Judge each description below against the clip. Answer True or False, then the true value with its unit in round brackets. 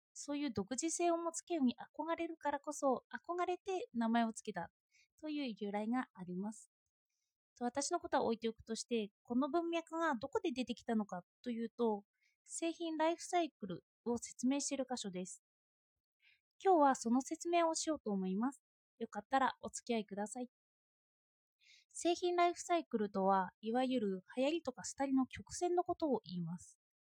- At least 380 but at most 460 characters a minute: False (340 characters per minute)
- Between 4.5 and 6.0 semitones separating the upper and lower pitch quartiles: False (6.7 semitones)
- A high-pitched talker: True (260 Hz)